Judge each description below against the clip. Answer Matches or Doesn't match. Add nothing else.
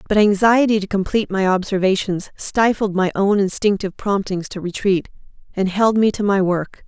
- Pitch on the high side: Matches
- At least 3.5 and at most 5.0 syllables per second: Doesn't match